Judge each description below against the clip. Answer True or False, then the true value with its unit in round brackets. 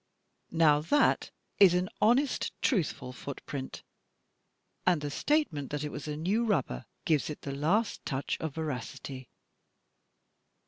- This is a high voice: False (155 Hz)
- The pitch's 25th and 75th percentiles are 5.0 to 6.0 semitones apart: True (5.4 semitones)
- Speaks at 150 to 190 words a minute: False (135 wpm)